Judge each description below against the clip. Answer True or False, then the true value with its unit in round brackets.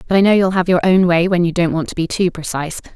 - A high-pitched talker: False (175 Hz)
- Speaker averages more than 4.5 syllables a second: True (6.8 syllables/s)